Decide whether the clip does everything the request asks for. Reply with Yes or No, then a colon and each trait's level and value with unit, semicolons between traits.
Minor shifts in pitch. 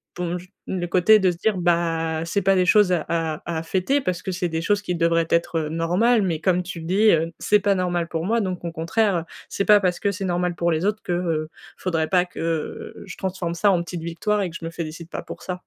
Yes: narrow, 2.3 semitones